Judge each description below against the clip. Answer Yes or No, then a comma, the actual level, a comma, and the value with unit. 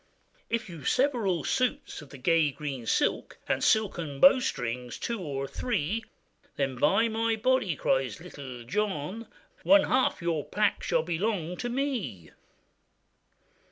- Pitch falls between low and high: Yes, medium, 180 Hz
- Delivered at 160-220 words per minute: No, average, 140 wpm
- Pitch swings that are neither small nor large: No, wide, 8.3 semitones